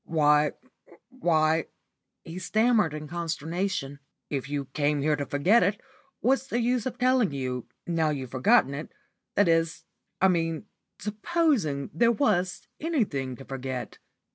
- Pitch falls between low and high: Yes, medium, 165 Hz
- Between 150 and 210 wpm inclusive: No, average, 140 wpm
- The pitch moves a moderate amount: No, wide, 6.9 semitones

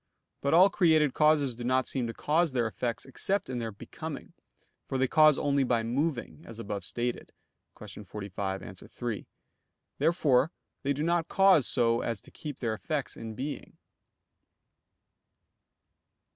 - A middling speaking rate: Yes, average, 150 wpm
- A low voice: Yes, low, 130 Hz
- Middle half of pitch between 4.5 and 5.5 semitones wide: Yes, average, 4.8 semitones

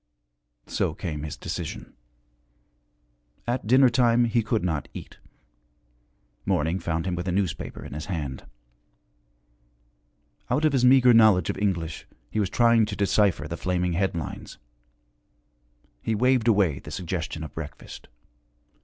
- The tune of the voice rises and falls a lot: Yes, wide, 6.0 semitones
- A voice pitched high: No, very low, 95 Hz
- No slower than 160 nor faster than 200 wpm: No, slow, 135 wpm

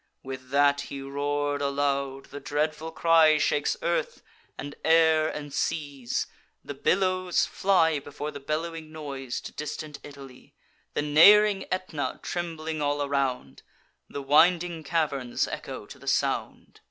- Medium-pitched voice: Yes, medium, 150 Hz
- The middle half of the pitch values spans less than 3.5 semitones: Yes, narrow, 2.5 semitones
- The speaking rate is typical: No, slow, 130 wpm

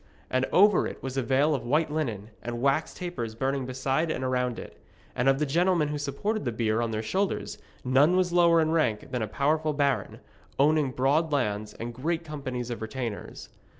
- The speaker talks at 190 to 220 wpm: Yes, average, 195 wpm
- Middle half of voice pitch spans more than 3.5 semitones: Yes, average, 4.3 semitones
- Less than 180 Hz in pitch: Yes, low, 135 Hz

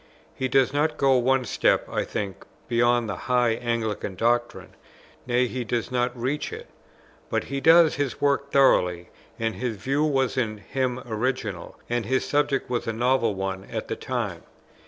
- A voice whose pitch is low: Yes, low, 125 Hz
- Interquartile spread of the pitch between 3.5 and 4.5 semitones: No, average, 2.9 semitones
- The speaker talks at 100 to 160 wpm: No, average, 170 wpm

